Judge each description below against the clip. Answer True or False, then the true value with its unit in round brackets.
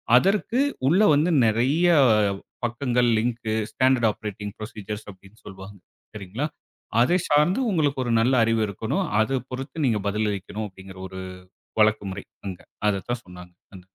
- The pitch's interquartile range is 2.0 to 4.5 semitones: False (4.9 semitones)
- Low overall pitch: True (110 Hz)